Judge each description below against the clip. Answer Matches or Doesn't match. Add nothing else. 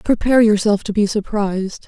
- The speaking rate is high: Doesn't match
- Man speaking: Doesn't match